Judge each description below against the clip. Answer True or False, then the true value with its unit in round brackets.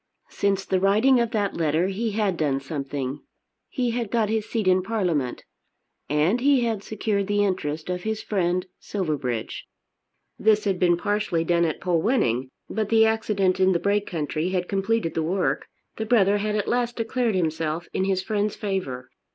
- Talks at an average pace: True (175 wpm)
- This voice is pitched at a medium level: False (195 Hz)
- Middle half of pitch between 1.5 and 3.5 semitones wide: False (4.5 semitones)